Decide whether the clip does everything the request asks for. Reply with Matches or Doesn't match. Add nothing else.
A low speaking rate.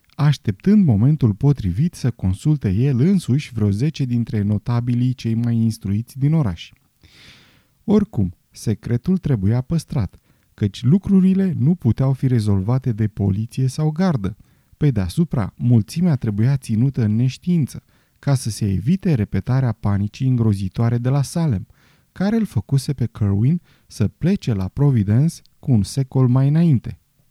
Doesn't match